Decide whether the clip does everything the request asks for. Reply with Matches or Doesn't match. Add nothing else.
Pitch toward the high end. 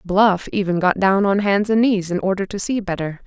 Matches